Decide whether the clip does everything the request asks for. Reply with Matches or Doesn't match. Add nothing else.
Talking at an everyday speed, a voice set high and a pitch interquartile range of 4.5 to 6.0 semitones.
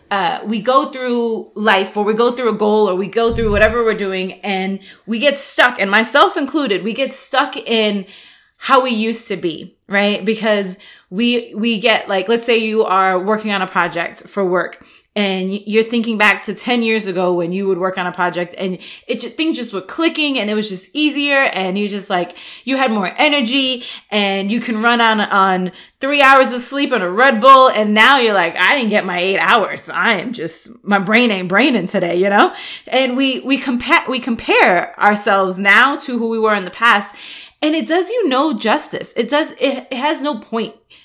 Doesn't match